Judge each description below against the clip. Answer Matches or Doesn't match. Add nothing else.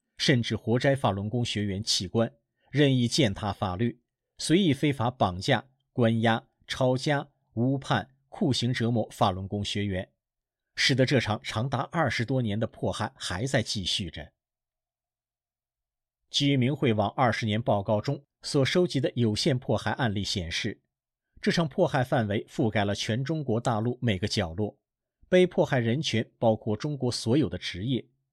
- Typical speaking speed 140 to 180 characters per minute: Doesn't match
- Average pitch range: Matches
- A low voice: Matches